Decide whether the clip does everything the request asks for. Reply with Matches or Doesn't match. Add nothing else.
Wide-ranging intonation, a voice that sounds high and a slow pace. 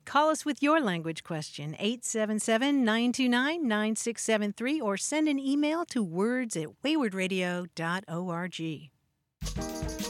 Matches